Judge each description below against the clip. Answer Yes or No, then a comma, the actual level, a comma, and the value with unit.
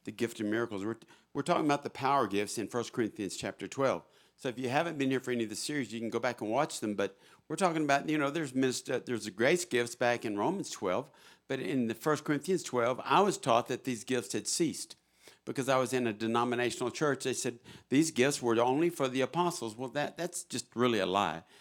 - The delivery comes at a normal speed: No, fast, 245 wpm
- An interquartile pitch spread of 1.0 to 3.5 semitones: No, average, 3.9 semitones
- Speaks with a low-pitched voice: Yes, low, 125 Hz